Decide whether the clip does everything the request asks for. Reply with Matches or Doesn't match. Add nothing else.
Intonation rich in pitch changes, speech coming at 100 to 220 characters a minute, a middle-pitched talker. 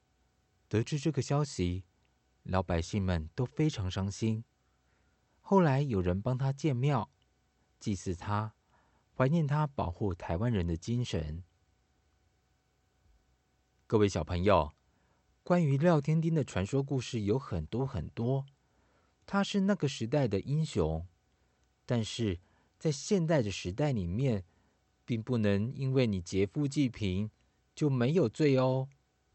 Doesn't match